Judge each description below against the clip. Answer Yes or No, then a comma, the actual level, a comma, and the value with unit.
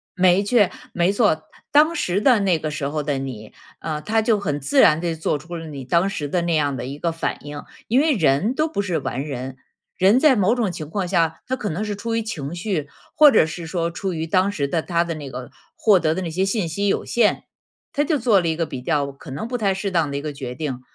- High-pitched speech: No, medium, 170 Hz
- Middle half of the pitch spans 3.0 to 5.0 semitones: No, wide, 5.4 semitones